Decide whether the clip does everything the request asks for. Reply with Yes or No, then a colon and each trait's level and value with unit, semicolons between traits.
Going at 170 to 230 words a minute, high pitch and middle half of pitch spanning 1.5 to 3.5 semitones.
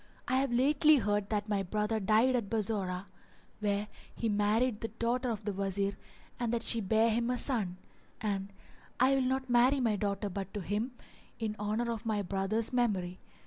Yes: average, 185 wpm; high, 215 Hz; average, 3.0 semitones